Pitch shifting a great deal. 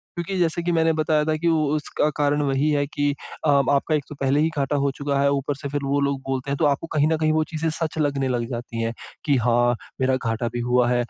No: narrow, 2.5 semitones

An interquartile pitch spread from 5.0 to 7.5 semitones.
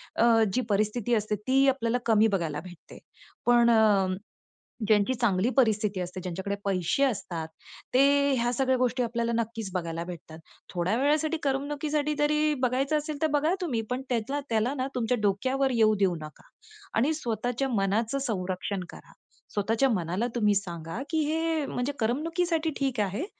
Yes: average, 5.3 semitones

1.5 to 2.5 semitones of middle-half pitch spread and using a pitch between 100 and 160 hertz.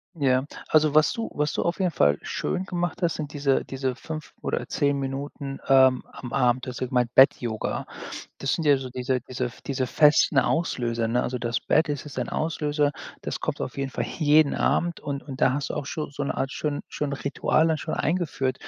No: average, 2.9 semitones; medium, 140 Hz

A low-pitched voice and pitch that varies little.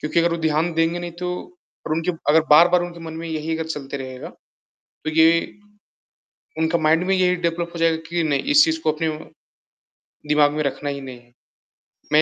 No: medium, 160 Hz; narrow, 2.1 semitones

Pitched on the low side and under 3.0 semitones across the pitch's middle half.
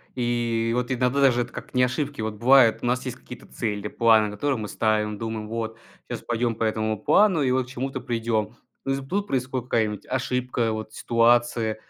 Yes: low, 120 Hz; narrow, 2.6 semitones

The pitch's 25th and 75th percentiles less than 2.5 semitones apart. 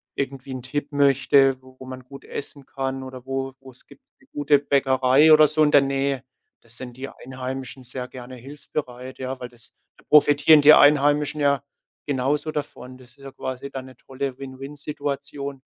Yes: narrow, 1.8 semitones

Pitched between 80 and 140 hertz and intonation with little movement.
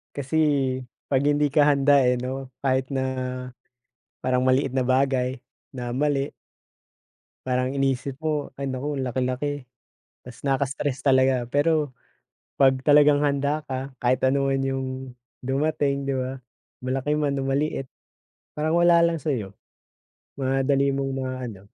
Yes: low, 135 Hz; narrow, 1.9 semitones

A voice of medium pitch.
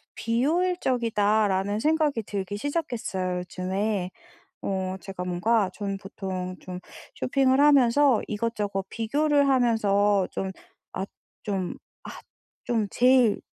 No: high, 210 Hz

